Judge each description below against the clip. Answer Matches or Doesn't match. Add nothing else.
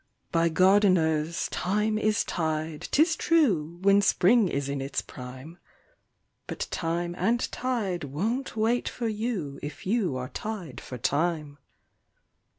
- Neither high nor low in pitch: Matches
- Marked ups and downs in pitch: Matches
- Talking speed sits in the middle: Doesn't match